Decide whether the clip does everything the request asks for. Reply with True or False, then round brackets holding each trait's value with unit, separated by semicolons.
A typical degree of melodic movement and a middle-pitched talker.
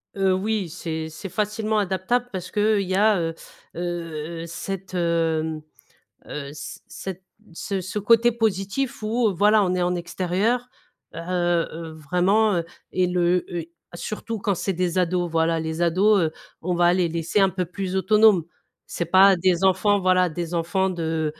True (3.0 semitones; 180 Hz)